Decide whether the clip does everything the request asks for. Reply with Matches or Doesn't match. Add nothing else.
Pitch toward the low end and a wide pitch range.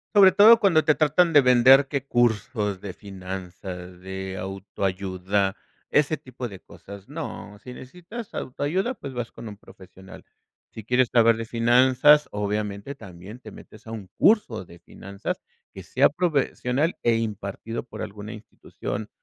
Matches